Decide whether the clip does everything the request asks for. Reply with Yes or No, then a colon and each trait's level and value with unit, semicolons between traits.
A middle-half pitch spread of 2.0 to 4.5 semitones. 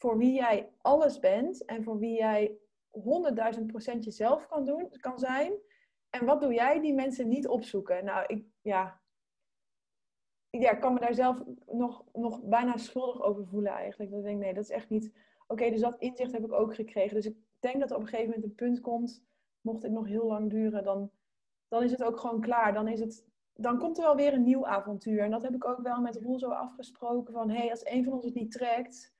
Yes: average, 2.8 semitones